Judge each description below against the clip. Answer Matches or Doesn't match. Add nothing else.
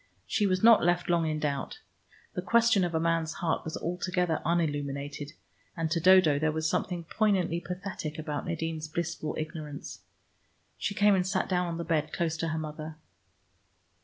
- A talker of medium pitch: Matches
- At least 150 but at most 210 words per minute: Matches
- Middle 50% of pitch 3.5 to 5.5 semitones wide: Doesn't match